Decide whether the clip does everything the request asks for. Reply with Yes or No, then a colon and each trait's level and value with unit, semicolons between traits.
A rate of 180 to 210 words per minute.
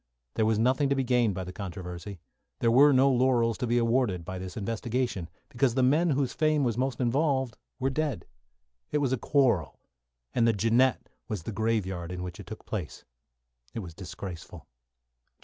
Yes: average, 185 wpm